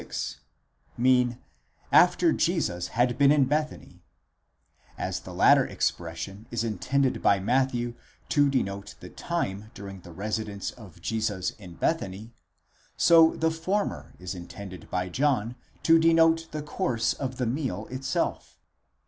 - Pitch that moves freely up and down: Yes, wide, 6.5 semitones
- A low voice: Yes, low, 120 Hz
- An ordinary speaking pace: No, slow, 130 wpm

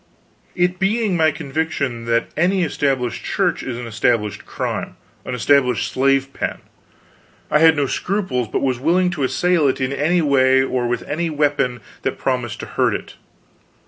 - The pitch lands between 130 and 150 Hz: Yes, medium, 140 Hz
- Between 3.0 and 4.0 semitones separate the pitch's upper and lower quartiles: No, average, 4.5 semitones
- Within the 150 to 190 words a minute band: Yes, average, 165 wpm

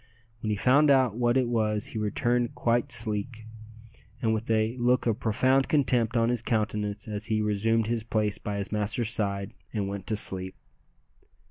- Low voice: Yes, low, 110 Hz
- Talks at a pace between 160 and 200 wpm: Yes, average, 175 wpm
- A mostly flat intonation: Yes, narrow, 2.3 semitones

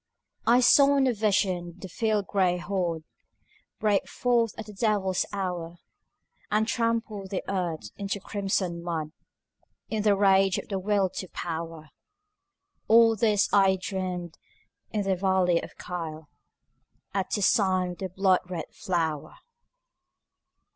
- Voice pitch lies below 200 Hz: Yes, high, 190 Hz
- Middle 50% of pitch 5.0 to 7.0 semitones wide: No, average, 2.9 semitones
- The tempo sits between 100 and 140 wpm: Yes, slow, 135 wpm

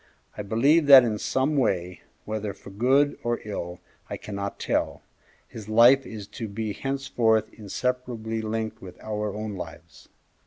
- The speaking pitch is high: No, low, 110 Hz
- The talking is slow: No, average, 150 wpm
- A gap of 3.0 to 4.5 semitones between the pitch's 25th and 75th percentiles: Yes, average, 3.7 semitones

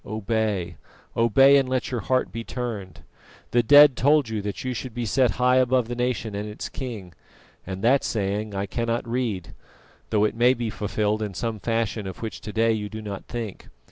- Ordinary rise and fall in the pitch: Yes, average, 3.1 semitones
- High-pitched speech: No, low, 115 Hz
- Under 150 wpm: No, average, 200 wpm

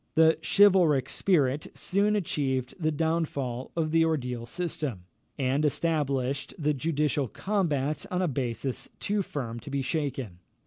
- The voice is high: No, medium, 150 Hz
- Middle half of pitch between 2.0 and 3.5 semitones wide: No, average, 3.9 semitones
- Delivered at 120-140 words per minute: Yes, slow, 135 wpm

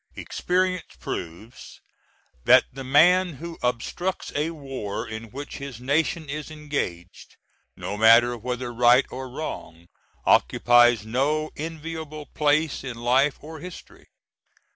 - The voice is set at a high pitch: No, medium, 140 Hz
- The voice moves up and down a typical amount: Yes, average, 4.5 semitones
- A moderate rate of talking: No, slow, 120 wpm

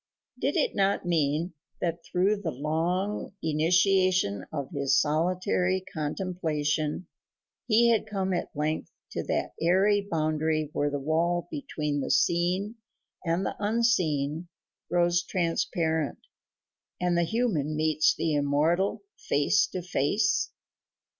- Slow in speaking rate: Yes, slow, 120 wpm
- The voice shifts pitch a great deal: No, average, 3.5 semitones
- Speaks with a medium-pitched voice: Yes, medium, 170 Hz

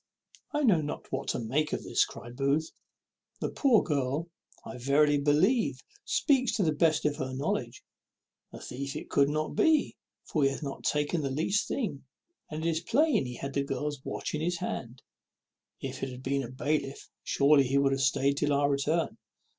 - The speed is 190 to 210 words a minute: Yes, average, 195 wpm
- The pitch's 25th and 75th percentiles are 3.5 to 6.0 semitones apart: No, average, 2.9 semitones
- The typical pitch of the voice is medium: Yes, medium, 145 Hz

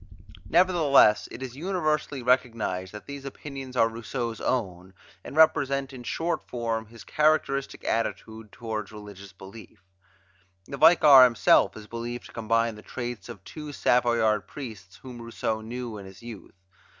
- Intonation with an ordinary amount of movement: Yes, average, 4.0 semitones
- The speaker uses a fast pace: No, average, 145 wpm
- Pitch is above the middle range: No, low, 120 Hz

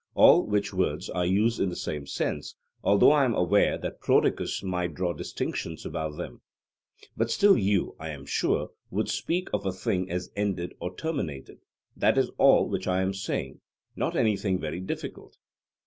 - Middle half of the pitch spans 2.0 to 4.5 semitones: Yes, average, 2.9 semitones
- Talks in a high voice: No, very low, 95 Hz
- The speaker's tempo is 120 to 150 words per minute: No, average, 175 wpm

